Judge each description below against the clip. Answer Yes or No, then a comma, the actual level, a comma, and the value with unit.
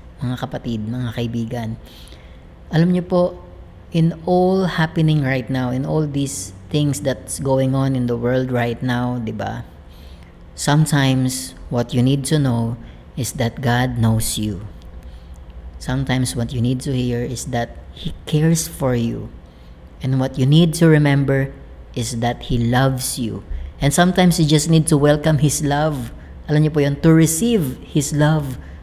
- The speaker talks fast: Yes, fast, 160 wpm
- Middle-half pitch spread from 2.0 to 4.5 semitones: No, average, 4.9 semitones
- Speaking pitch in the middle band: No, low, 125 Hz